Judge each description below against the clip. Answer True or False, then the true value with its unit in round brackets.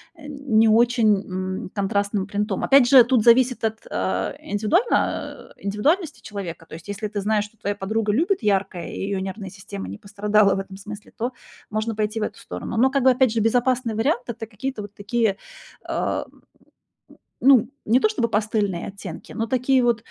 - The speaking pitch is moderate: False (215 Hz)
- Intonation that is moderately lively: True (3.1 semitones)